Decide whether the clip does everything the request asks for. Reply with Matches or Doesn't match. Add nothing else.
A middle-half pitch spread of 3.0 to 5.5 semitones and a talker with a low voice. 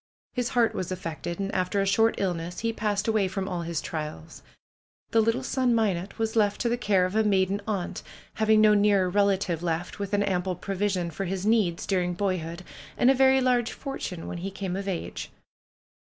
Doesn't match